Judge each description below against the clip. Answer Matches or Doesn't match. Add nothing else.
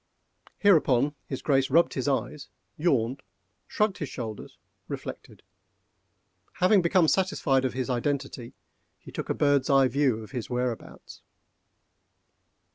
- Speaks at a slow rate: Matches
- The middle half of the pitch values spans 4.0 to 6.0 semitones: Doesn't match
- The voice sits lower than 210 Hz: Matches